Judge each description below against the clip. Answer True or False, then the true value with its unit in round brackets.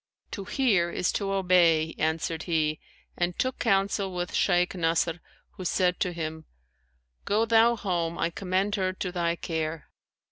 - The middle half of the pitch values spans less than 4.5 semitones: True (2.8 semitones)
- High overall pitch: False (180 Hz)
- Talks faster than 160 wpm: False (150 wpm)